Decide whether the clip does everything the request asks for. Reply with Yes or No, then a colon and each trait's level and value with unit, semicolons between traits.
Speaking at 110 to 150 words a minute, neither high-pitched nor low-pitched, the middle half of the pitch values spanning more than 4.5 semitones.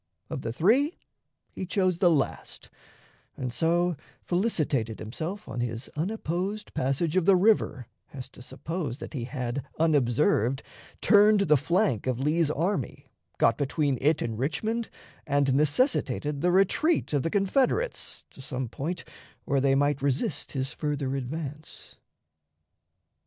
Yes: slow, 135 wpm; medium, 150 Hz; wide, 5.6 semitones